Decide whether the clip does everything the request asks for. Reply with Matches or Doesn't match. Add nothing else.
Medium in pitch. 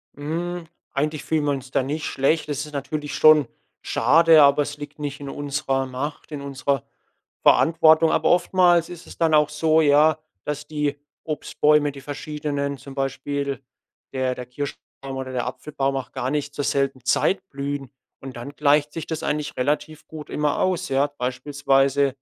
Matches